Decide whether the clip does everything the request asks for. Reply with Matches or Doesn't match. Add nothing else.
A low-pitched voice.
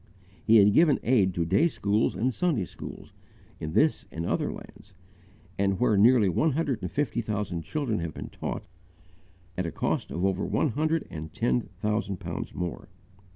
Matches